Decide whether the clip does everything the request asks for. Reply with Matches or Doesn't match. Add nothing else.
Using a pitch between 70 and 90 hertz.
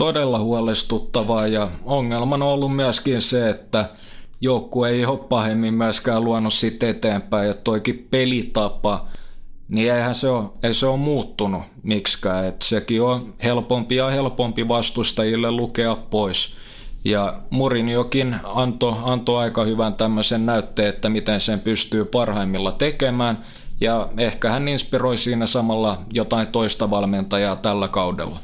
Doesn't match